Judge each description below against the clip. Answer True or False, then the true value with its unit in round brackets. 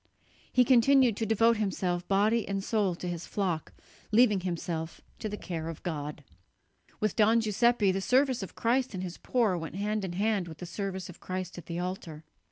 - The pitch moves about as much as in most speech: True (4.1 semitones)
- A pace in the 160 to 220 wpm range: True (190 wpm)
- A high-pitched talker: True (195 Hz)